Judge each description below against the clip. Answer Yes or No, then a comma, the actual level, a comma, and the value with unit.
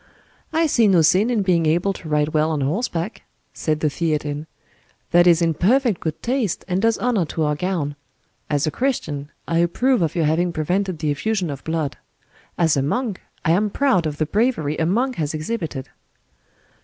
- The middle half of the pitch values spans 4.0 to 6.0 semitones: Yes, average, 5.2 semitones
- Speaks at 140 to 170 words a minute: No, average, 190 wpm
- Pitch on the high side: No, medium, 170 Hz